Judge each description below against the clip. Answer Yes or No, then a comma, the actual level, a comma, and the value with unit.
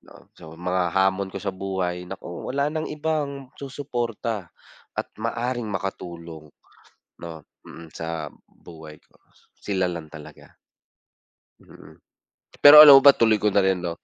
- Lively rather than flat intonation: Yes, wide, 6.0 semitones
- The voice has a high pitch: No, very low, 95 Hz